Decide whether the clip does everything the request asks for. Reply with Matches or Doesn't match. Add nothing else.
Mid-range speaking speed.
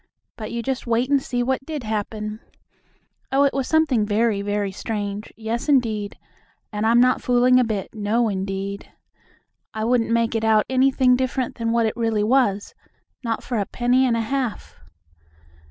Matches